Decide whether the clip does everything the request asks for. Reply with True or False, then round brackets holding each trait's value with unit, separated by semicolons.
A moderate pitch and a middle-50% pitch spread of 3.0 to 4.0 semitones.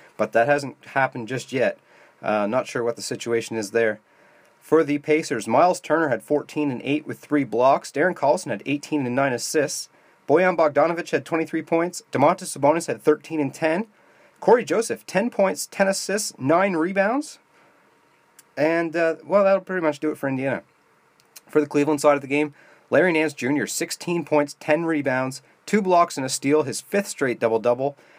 True (150 Hz; 3.5 semitones)